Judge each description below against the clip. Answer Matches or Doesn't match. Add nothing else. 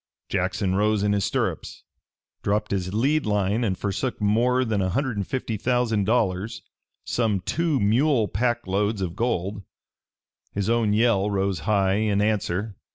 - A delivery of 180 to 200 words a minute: Doesn't match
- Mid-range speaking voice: Doesn't match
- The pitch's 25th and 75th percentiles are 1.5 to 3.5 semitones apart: Matches